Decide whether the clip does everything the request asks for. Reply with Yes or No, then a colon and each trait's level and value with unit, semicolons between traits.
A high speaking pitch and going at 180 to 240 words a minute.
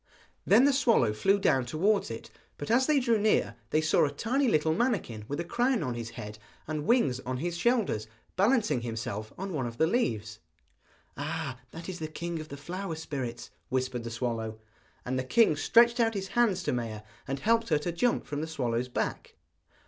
No: medium, 155 Hz; average, 200 wpm